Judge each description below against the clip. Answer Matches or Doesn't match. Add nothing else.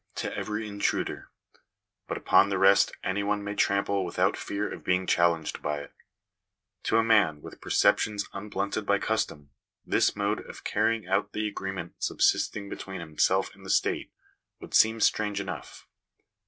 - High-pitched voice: Doesn't match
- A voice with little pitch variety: Matches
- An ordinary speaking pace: Matches